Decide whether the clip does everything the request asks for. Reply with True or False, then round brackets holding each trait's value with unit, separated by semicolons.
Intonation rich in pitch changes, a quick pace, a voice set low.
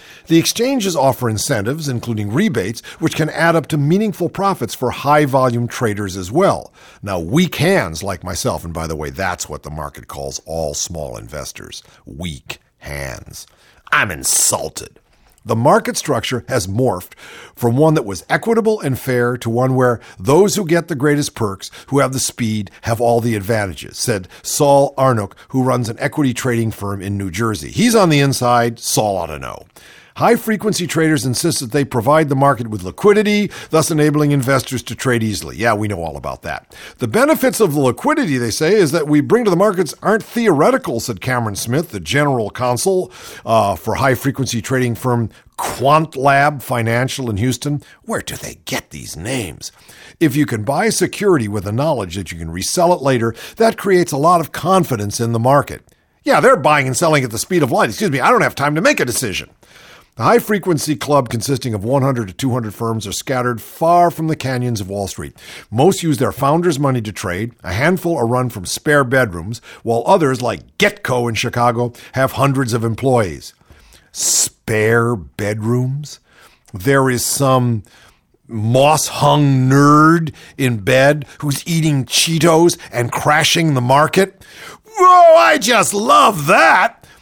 False (5.7 semitones; 180 wpm; 130 Hz)